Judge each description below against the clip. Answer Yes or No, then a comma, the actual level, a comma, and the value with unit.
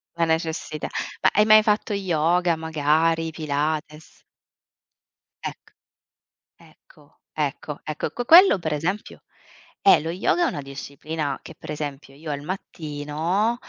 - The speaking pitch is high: No, medium, 160 Hz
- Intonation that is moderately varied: Yes, average, 3.2 semitones